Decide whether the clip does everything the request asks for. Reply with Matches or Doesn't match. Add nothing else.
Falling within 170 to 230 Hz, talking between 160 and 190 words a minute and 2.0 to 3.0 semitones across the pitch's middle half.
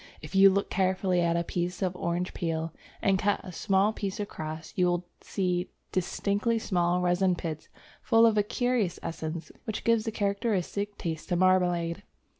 Matches